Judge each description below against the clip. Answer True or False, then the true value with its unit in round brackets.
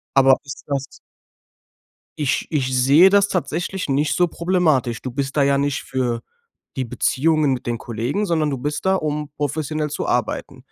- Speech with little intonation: False (3.1 semitones)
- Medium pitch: True (145 Hz)